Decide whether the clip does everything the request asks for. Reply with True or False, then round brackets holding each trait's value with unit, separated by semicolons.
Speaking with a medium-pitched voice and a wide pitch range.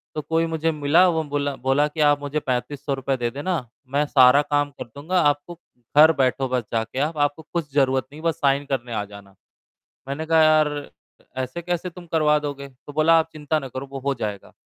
False (145 Hz; 2.8 semitones)